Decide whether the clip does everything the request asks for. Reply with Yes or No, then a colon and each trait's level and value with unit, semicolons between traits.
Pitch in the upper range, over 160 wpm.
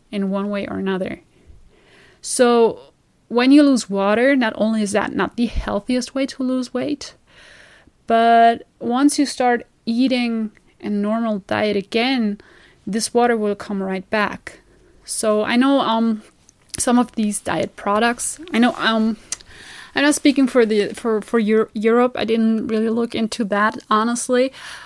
No: high, 230 Hz; average, 155 wpm